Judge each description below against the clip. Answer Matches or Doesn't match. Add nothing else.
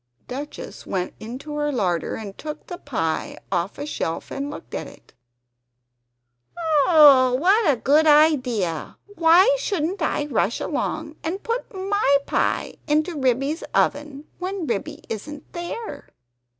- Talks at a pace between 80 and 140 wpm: Matches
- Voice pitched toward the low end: Doesn't match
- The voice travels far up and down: Doesn't match